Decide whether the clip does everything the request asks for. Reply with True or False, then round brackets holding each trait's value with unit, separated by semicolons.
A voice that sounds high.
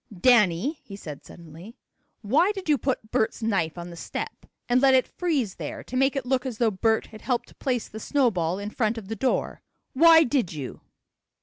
True (230 Hz)